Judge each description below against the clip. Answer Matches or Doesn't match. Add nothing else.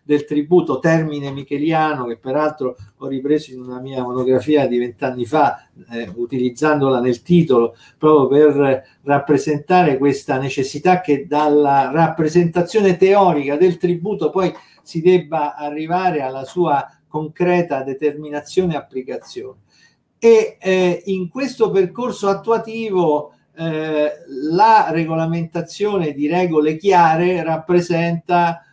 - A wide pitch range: Doesn't match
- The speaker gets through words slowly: Matches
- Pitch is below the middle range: Doesn't match